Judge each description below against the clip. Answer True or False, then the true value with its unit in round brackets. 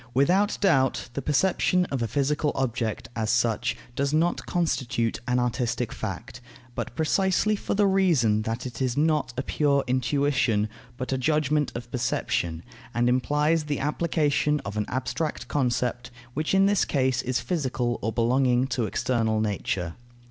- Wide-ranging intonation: False (4.0 semitones)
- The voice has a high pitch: False (130 Hz)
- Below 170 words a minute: True (155 wpm)